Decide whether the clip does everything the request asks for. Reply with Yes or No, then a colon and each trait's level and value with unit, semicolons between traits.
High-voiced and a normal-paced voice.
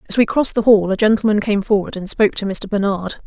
No: high, 205 Hz; fast, 255 wpm